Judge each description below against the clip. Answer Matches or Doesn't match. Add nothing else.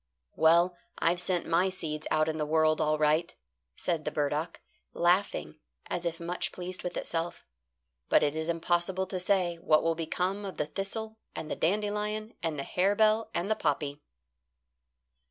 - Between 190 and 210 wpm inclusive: Doesn't match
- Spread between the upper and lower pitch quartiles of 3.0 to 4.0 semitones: Matches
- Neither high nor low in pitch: Matches